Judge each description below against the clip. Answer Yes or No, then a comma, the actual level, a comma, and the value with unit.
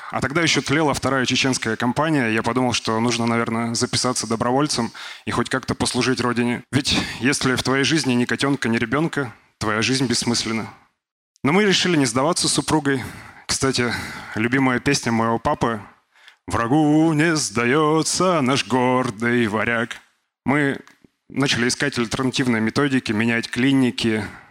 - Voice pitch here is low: Yes, low, 125 Hz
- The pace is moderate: Yes, average, 135 wpm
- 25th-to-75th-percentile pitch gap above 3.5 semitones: No, average, 3.2 semitones